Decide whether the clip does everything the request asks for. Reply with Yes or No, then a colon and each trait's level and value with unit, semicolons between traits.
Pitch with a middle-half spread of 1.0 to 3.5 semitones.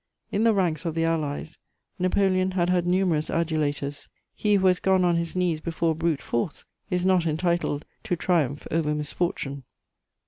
Yes: average, 2.9 semitones